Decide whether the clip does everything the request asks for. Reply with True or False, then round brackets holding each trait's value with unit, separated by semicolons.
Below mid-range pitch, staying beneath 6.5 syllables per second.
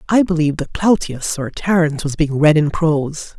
False (160 Hz; 5.3 syllables/s)